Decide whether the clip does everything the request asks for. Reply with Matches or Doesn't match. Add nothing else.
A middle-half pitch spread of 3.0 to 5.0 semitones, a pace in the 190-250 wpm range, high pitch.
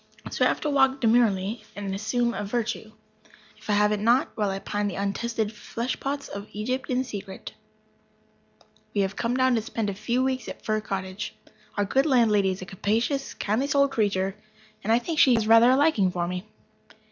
Matches